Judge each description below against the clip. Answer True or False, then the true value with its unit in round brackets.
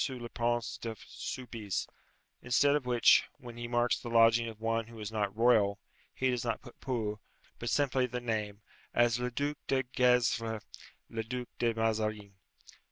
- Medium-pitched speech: False (115 Hz)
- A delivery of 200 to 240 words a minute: False (165 wpm)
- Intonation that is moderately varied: False (1.8 semitones)